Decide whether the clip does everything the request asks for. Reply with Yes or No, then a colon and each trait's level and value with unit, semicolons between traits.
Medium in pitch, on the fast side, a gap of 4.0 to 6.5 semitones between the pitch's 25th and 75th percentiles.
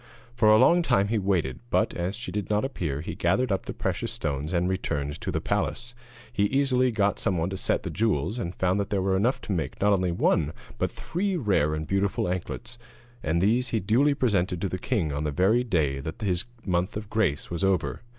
No: very low, 95 Hz; fast, 225 wpm; average, 4.7 semitones